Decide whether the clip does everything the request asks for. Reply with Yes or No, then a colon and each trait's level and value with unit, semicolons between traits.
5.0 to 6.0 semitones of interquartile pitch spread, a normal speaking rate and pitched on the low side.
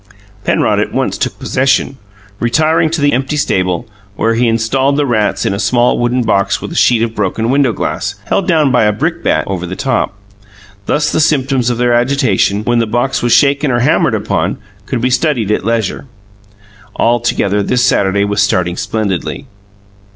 No: average, 4.1 semitones; average, 180 wpm; low, 120 Hz